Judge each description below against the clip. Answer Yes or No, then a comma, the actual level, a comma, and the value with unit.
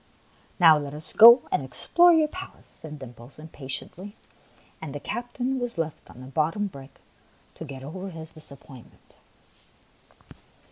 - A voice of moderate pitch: Yes, medium, 160 Hz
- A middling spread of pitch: No, wide, 7.0 semitones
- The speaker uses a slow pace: No, average, 145 wpm